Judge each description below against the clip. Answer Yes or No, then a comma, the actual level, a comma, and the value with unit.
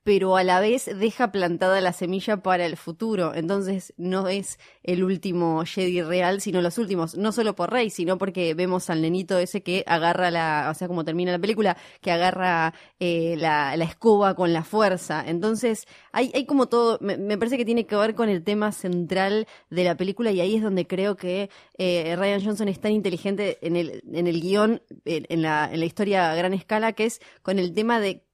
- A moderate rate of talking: No, fast, 210 wpm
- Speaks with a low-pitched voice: No, medium, 185 Hz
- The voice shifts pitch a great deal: No, average, 3.2 semitones